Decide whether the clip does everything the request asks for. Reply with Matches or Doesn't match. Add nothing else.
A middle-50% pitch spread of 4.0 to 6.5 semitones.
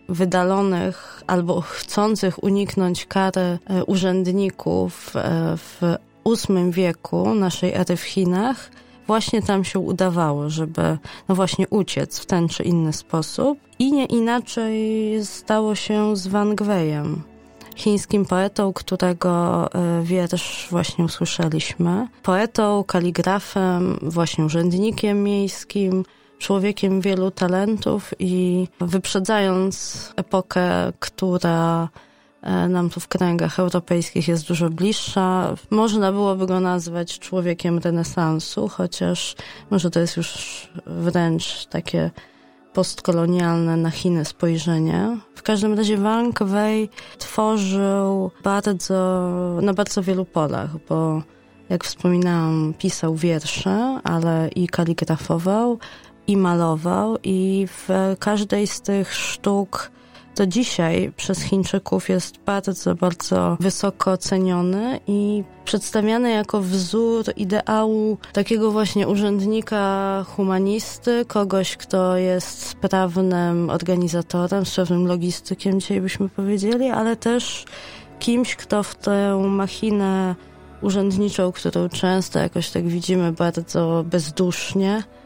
Doesn't match